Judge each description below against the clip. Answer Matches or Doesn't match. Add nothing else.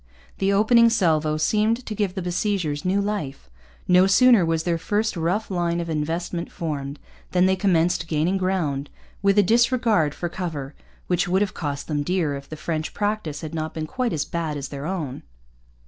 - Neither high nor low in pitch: Matches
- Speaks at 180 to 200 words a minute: Matches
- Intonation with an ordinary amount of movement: Matches